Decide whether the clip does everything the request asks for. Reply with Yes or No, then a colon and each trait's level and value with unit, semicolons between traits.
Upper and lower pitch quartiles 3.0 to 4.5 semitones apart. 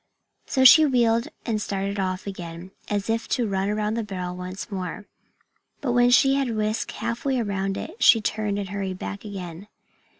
Yes: average, 3.3 semitones